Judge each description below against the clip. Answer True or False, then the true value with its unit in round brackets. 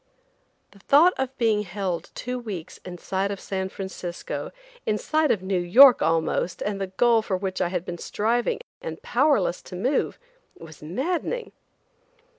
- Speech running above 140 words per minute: True (160 wpm)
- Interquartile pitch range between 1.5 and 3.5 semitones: False (5.1 semitones)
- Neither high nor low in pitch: False (195 Hz)